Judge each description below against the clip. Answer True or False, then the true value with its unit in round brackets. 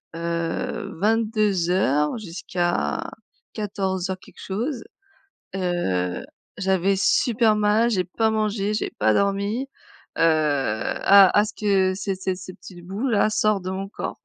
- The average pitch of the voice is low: False (195 Hz)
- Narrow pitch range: False (3.1 semitones)